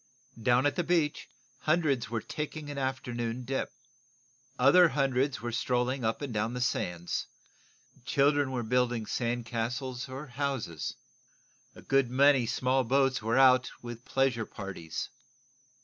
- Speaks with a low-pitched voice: Yes, low, 125 Hz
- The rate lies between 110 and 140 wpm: Yes, slow, 135 wpm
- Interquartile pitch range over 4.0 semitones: No, narrow, 2.6 semitones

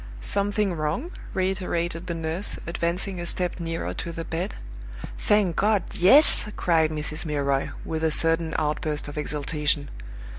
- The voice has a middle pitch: Yes, medium, 165 Hz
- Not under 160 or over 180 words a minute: No, average, 140 wpm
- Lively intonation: No, average, 3.2 semitones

